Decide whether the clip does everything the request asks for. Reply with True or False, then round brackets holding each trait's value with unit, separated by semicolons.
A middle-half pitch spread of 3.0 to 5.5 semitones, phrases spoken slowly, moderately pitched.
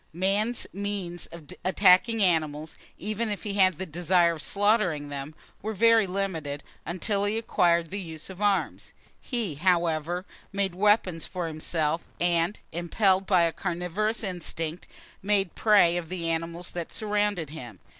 False (3.6 semitones; 145 wpm; 180 Hz)